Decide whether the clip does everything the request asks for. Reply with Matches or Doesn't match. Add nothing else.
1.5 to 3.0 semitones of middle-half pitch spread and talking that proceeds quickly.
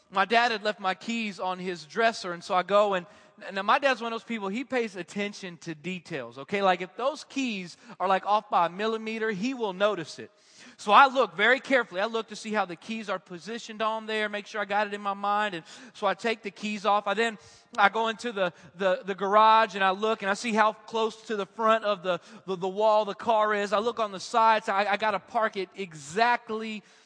Matches